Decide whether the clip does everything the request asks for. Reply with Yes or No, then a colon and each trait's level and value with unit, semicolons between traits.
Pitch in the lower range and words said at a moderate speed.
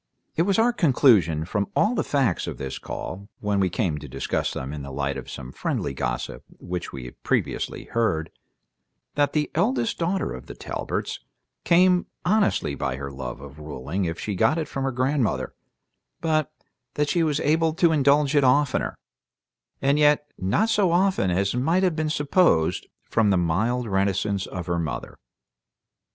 Yes: low, 115 Hz; average, 175 wpm